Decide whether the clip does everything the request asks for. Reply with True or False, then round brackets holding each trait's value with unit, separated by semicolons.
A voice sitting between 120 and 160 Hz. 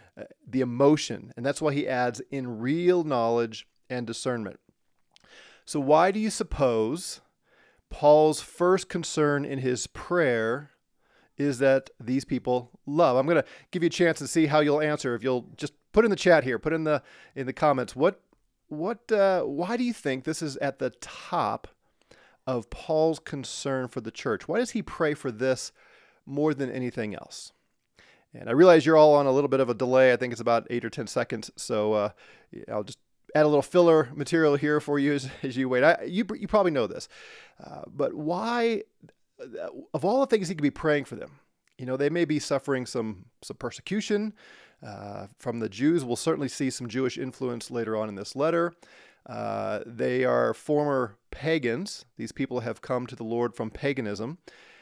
True (140 Hz)